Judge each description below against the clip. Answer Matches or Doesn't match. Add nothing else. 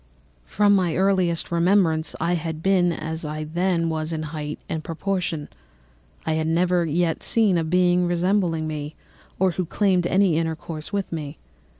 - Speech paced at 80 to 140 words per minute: Doesn't match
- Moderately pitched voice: Matches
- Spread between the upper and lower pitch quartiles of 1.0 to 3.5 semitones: Matches